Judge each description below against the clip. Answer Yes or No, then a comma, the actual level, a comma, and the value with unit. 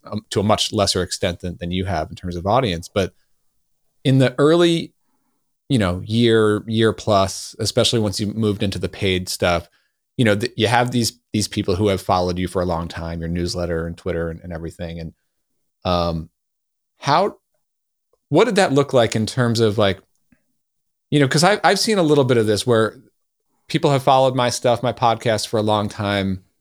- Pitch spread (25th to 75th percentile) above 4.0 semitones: Yes, average, 5.2 semitones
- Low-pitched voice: Yes, low, 105 Hz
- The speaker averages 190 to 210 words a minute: Yes, average, 200 wpm